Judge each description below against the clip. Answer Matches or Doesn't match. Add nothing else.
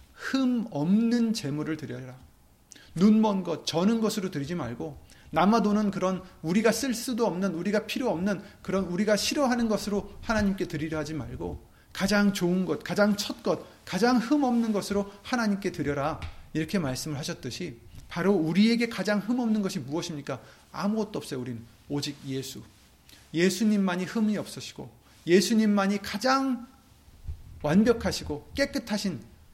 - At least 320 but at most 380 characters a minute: Matches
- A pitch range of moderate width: Doesn't match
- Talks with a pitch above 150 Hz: Matches